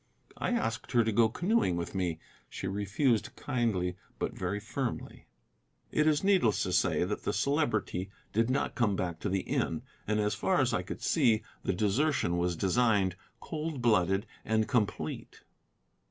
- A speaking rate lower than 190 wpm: Yes, average, 165 wpm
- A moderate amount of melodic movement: Yes, average, 4.8 semitones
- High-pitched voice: No, low, 110 Hz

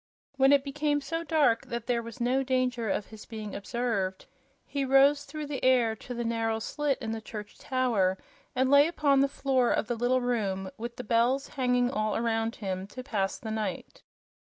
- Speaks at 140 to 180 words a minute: No, average, 195 wpm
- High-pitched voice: Yes, high, 245 Hz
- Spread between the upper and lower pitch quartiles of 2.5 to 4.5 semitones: Yes, average, 3.5 semitones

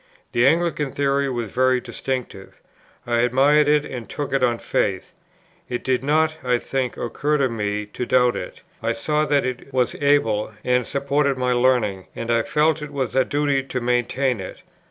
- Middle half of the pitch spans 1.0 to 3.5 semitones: Yes, average, 2.9 semitones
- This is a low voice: Yes, low, 130 Hz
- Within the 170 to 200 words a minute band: Yes, average, 180 wpm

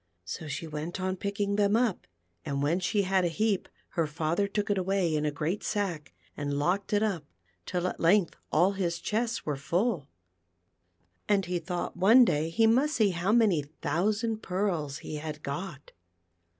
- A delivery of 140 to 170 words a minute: No, average, 180 wpm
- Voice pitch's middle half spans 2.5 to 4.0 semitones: No, average, 4.6 semitones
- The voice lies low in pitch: No, medium, 185 Hz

